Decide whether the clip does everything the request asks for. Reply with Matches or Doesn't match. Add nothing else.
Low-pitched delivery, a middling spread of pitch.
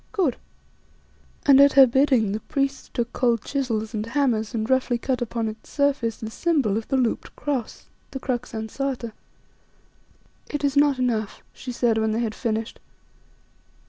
Doesn't match